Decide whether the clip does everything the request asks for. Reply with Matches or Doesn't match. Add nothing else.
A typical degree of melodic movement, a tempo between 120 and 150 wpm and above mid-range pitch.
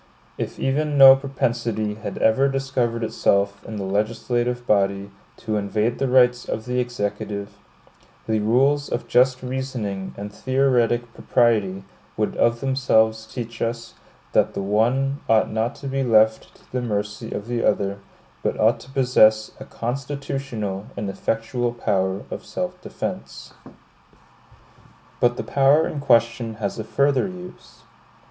Doesn't match